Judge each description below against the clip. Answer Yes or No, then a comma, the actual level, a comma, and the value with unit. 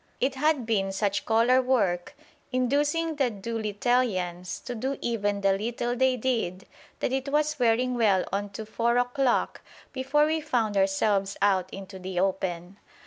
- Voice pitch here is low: No, high, 230 Hz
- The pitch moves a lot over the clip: No, average, 4.9 semitones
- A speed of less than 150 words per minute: No, average, 155 wpm